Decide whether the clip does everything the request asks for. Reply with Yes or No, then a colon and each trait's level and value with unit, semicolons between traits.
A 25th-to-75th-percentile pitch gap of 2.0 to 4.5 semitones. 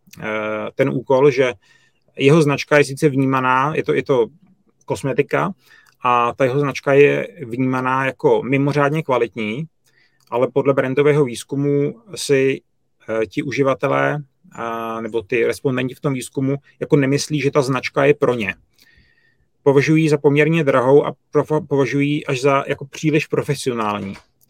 Yes: narrow, 2.4 semitones